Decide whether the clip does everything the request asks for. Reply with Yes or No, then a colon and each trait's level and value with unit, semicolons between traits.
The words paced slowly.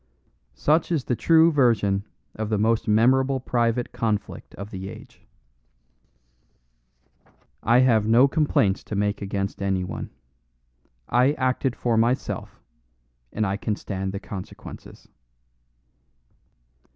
Yes: slow, 115 wpm